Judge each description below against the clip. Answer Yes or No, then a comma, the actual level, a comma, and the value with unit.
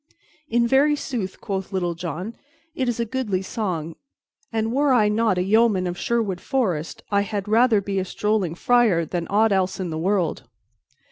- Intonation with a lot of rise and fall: No, average, 4.2 semitones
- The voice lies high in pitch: Yes, high, 205 Hz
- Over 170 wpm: Yes, average, 180 wpm